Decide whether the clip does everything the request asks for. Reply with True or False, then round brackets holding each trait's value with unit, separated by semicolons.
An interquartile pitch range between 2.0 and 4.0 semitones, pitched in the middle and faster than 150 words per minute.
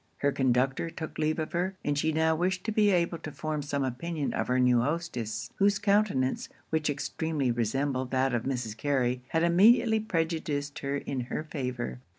False (4.6 semitones; 145 Hz; 180 wpm)